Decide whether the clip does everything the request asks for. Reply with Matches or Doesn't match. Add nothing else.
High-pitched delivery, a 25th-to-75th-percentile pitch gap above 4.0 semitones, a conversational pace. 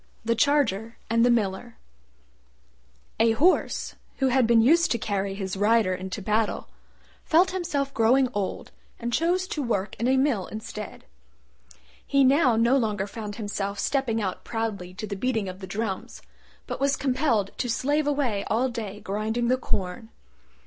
Matches